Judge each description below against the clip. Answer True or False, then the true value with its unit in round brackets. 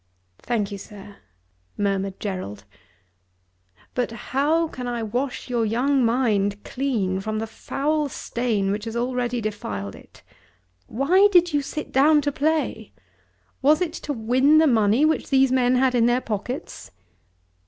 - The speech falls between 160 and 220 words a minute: False (145 wpm)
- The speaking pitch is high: True (245 Hz)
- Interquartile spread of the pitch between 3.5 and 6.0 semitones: True (4.7 semitones)